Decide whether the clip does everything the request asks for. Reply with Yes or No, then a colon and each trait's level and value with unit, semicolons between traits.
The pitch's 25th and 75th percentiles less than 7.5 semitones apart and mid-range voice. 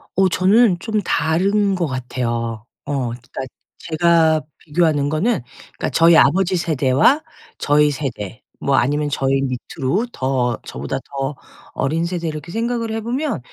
Yes: wide, 5.6 semitones; medium, 155 Hz